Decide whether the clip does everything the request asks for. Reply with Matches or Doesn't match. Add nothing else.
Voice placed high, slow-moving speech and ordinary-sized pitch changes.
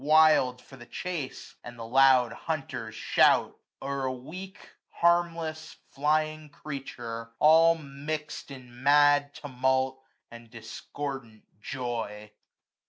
Doesn't match